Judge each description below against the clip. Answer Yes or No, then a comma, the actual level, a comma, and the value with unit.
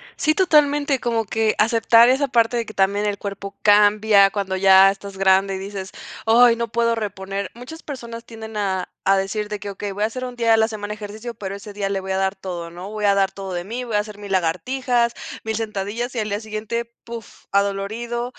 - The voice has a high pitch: Yes, high, 210 Hz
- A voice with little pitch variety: No, average, 3.0 semitones